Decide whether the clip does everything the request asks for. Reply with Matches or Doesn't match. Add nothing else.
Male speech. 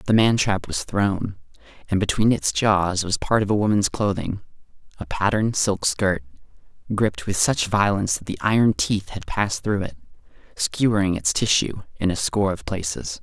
Matches